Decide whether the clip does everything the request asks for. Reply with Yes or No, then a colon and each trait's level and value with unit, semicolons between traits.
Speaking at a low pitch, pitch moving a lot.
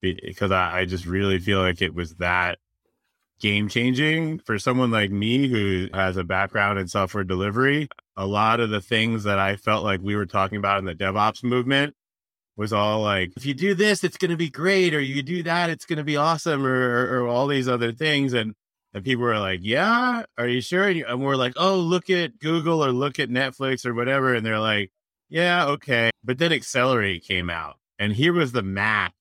Yes: low, 120 Hz; wide, 6.5 semitones